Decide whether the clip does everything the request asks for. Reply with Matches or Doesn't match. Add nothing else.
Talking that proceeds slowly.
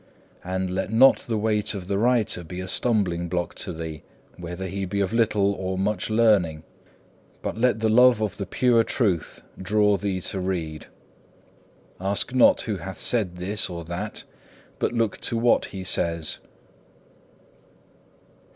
Doesn't match